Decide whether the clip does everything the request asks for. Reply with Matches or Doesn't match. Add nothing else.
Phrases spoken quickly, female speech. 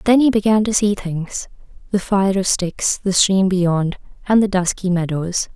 Doesn't match